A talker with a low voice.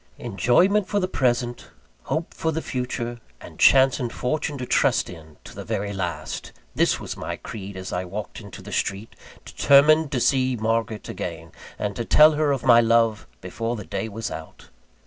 Yes: low, 120 Hz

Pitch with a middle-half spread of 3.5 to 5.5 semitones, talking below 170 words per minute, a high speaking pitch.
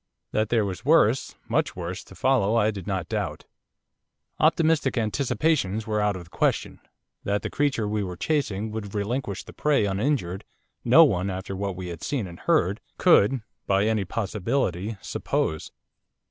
No: average, 4.9 semitones; average, 160 wpm; low, 105 Hz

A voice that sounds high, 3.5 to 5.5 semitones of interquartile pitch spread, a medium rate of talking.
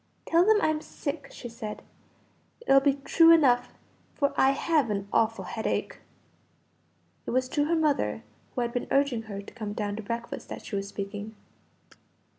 Yes: very high, 250 Hz; average, 5.2 semitones; average, 170 wpm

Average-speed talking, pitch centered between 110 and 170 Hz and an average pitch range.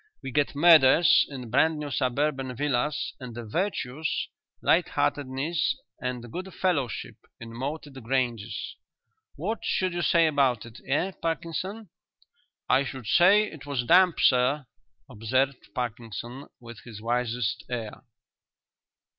No: slow, 125 wpm; low, 135 Hz; average, 4.6 semitones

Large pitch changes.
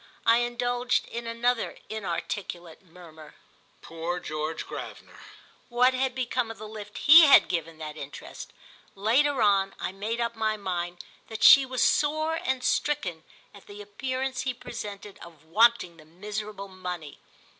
Yes: wide, 5.7 semitones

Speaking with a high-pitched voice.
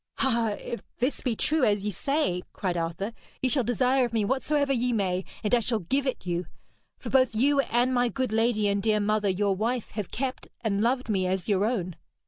Yes: high, 225 Hz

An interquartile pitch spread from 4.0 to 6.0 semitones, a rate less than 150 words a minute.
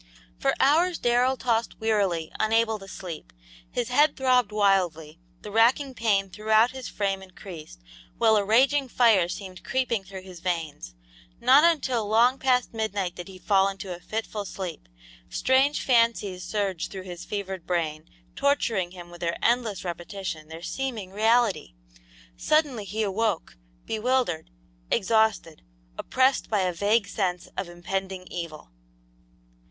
Yes: average, 4.6 semitones; average, 140 wpm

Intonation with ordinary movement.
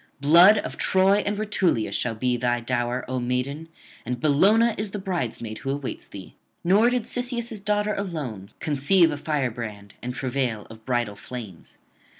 No: wide, 8.5 semitones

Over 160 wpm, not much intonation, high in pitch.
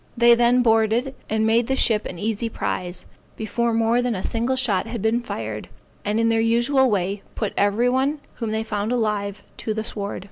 Yes: average, 200 wpm; narrow, 2.3 semitones; high, 225 Hz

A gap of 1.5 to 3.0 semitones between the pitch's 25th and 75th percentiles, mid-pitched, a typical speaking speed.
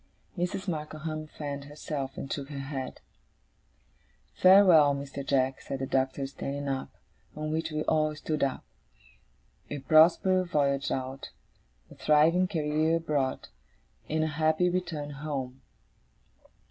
No: narrow, 2.4 semitones; medium, 150 Hz; slow, 125 wpm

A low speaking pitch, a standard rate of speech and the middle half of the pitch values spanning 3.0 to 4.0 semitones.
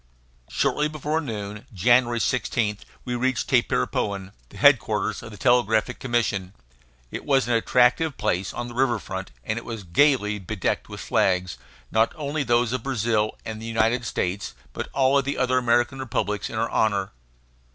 Yes: low, 115 Hz; average, 165 wpm; average, 3.6 semitones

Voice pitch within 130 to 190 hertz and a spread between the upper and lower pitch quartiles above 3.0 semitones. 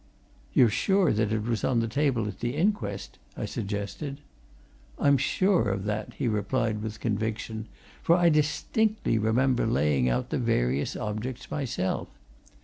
No: low, 115 Hz; average, 4.8 semitones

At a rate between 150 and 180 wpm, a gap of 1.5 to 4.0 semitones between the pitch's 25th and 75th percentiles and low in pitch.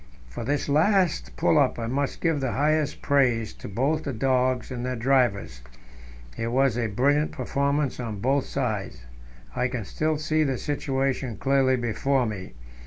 Yes: average, 165 wpm; average, 3.3 semitones; low, 130 Hz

